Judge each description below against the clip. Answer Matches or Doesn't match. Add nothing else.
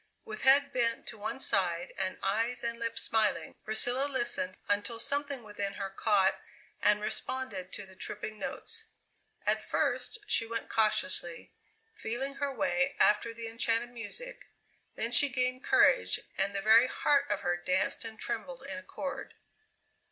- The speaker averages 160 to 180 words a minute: Doesn't match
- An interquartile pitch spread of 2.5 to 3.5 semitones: Doesn't match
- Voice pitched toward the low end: Doesn't match